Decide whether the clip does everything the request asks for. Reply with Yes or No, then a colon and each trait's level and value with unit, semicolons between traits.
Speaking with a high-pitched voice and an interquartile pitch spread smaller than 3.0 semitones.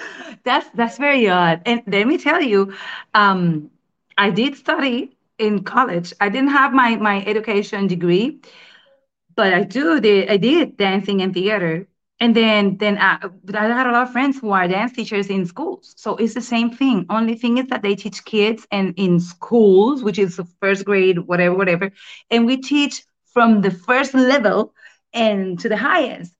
No: high, 215 Hz; average, 4.3 semitones